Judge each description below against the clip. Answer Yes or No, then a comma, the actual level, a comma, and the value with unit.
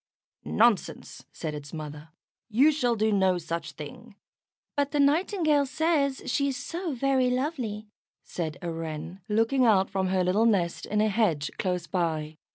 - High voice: Yes, high, 210 Hz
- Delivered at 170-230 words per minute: No, average, 160 wpm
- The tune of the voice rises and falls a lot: Yes, wide, 8.2 semitones